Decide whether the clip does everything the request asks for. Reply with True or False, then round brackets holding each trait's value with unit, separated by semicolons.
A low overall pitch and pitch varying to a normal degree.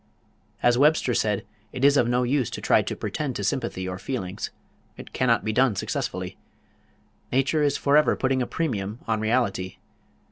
True (125 Hz; 4.1 semitones)